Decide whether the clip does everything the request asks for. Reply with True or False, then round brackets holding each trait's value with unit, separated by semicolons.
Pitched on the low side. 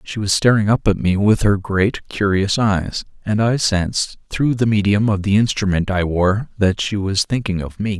True (100 Hz)